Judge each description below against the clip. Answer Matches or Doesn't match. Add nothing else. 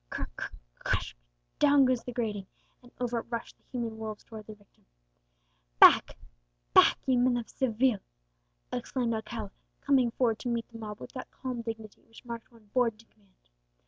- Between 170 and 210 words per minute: Matches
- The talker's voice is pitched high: Matches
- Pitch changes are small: Matches